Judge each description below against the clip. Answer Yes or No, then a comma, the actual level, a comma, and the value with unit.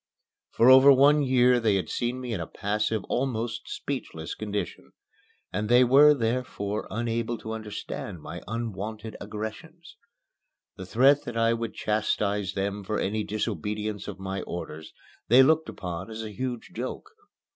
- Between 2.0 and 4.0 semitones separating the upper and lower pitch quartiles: Yes, average, 3.4 semitones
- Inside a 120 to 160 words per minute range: Yes, average, 150 wpm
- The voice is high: No, low, 110 Hz